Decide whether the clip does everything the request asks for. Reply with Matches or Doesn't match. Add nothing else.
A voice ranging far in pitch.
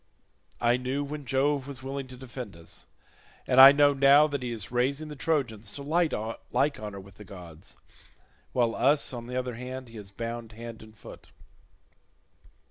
Doesn't match